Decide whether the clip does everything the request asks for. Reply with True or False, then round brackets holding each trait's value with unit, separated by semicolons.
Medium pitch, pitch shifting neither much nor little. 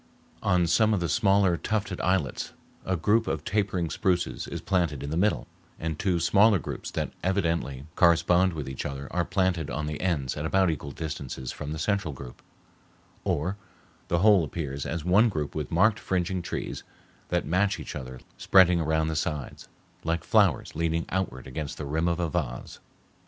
False (85 Hz; 3.8 semitones)